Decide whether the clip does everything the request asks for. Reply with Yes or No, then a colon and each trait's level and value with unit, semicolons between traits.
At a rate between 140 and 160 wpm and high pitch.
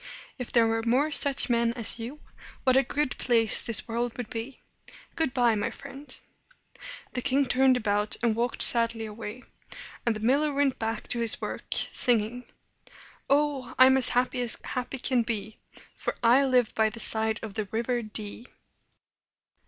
No: average, 170 wpm; high, 240 Hz